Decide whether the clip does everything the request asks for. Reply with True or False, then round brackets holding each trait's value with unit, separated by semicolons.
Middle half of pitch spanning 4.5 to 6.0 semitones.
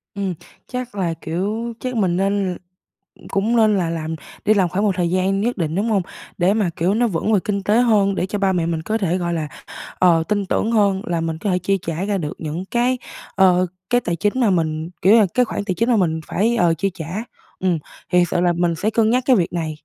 False (3.8 semitones)